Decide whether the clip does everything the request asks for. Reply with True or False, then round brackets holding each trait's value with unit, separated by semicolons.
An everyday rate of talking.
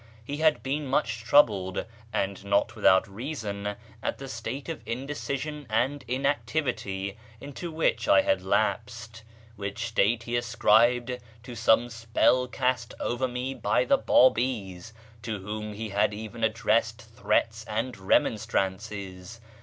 False (130 wpm)